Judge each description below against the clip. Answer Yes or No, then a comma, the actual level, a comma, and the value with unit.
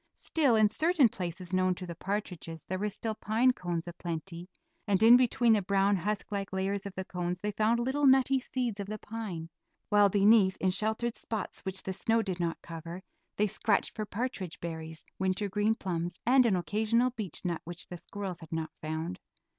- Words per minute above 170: Yes, average, 190 wpm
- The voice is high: Yes, high, 195 Hz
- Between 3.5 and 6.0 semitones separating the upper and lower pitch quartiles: Yes, average, 3.8 semitones